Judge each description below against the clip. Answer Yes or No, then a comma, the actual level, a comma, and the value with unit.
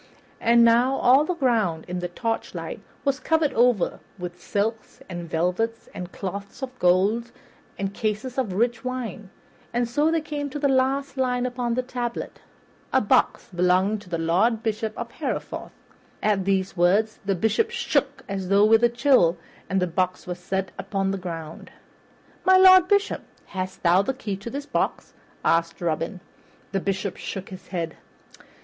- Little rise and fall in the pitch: No, wide, 5.6 semitones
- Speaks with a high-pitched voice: Yes, high, 215 Hz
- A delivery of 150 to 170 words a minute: Yes, average, 165 wpm